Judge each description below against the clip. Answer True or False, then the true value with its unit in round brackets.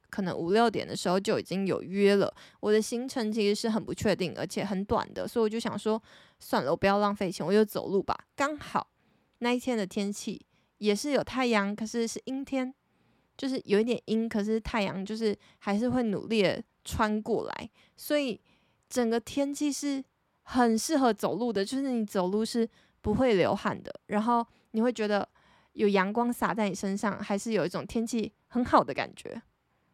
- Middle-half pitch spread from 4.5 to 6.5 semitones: False (3.0 semitones)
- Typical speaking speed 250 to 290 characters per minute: True (275 characters per minute)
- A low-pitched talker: False (220 Hz)